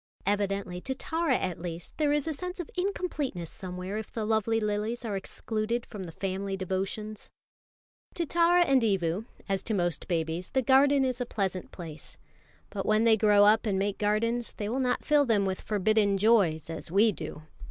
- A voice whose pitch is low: No, high, 210 Hz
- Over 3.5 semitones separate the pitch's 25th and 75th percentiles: Yes, average, 4.3 semitones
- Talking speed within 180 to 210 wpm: Yes, average, 190 wpm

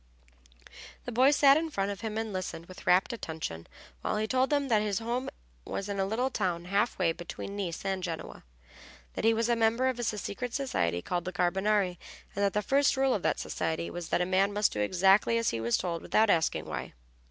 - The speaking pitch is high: Yes, high, 200 Hz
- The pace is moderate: No, fast, 220 wpm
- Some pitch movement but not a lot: Yes, average, 4.5 semitones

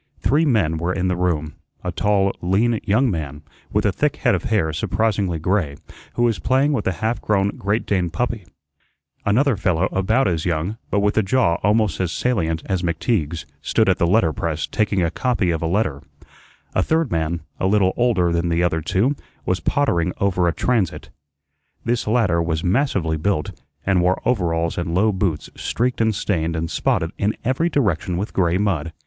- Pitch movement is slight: No, average, 4.6 semitones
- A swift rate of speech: No, average, 190 wpm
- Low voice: Yes, very low, 95 Hz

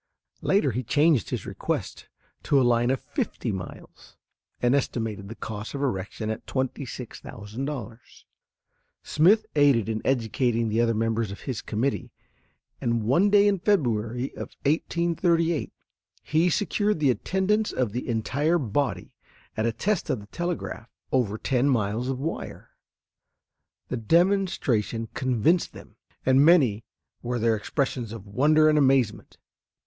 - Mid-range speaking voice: No, low, 130 Hz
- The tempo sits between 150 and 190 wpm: No, slow, 135 wpm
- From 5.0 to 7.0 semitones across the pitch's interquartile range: Yes, wide, 5.5 semitones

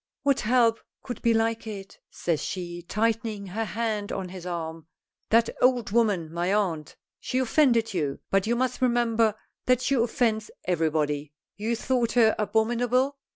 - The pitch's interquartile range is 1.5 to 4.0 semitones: No, average, 4.5 semitones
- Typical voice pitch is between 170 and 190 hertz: No, high, 220 Hz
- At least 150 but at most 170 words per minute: Yes, average, 155 wpm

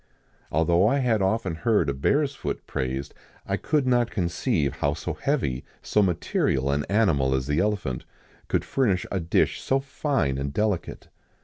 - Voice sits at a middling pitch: No, very low, 90 Hz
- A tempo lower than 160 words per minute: No, average, 165 wpm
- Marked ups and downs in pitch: Yes, wide, 8.6 semitones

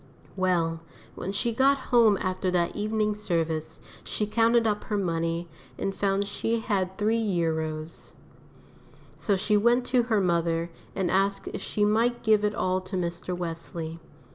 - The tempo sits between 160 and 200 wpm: No, average, 150 wpm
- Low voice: No, high, 195 Hz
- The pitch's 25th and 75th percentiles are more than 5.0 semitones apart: No, average, 3.9 semitones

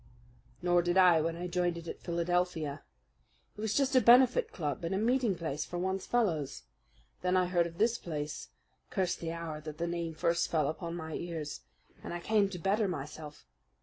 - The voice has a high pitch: No, medium, 175 Hz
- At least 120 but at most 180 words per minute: No, average, 195 wpm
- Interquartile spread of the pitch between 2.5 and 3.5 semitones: Yes, average, 2.8 semitones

